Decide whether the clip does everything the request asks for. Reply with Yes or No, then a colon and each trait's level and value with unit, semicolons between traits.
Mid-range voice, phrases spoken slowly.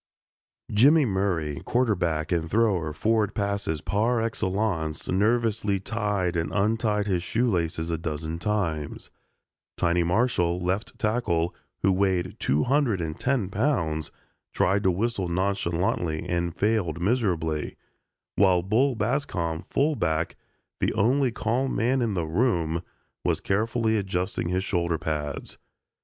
No: very low, 95 Hz; slow, 125 wpm